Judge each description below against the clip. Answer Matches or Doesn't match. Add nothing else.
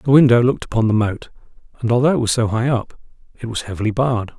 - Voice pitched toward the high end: Doesn't match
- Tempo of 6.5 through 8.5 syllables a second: Matches